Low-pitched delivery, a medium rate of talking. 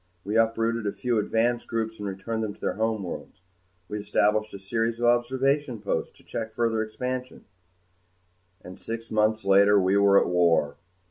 Yes: low, 110 Hz; average, 165 wpm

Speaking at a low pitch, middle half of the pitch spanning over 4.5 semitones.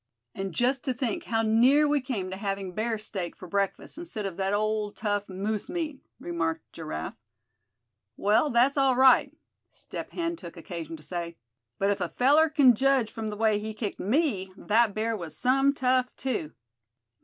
No: high, 215 Hz; average, 5.1 semitones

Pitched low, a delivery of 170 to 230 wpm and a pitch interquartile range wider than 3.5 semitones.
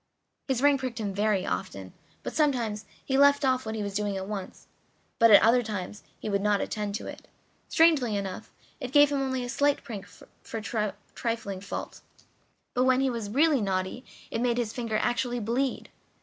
No: high, 230 Hz; average, 190 wpm; average, 4.1 semitones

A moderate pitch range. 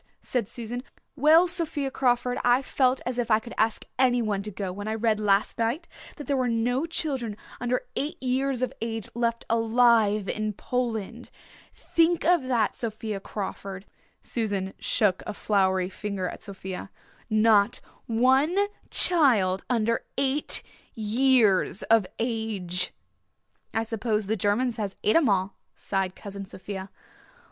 Yes: average, 3.7 semitones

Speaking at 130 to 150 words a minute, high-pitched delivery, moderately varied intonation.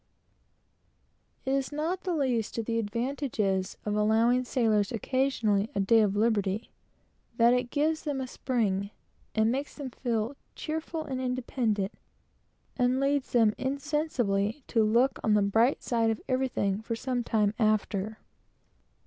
Yes: average, 140 wpm; high, 235 Hz; average, 3.8 semitones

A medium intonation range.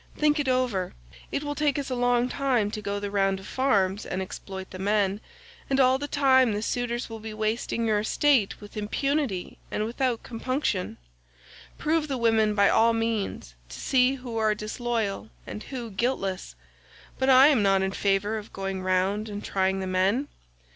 Yes: average, 4.5 semitones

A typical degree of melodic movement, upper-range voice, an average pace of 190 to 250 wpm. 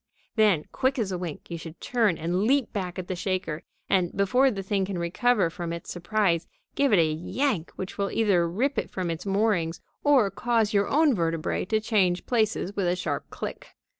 Yes: average, 4.3 semitones; high, 195 Hz; average, 200 wpm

